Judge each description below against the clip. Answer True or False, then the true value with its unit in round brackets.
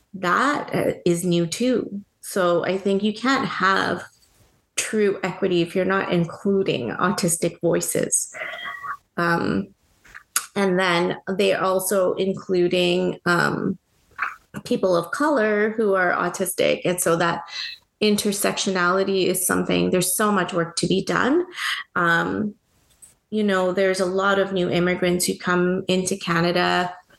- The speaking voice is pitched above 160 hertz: True (185 Hz)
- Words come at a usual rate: False (130 wpm)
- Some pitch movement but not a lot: False (2.2 semitones)